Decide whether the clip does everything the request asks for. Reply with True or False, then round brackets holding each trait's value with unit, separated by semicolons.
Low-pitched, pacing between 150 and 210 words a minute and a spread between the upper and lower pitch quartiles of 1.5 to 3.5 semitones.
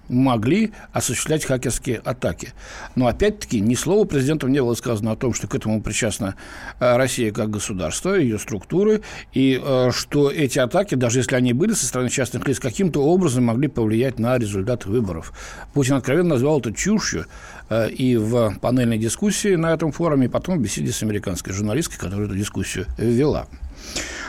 False (125 Hz; 160 wpm; 4.3 semitones)